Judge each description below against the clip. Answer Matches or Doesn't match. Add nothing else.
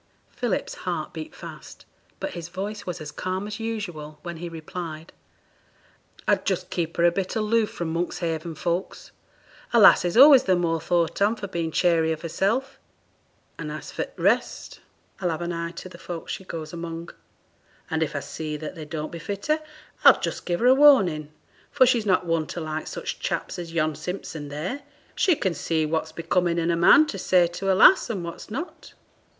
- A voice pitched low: Doesn't match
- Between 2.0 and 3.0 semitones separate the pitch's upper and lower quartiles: Doesn't match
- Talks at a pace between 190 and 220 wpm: Matches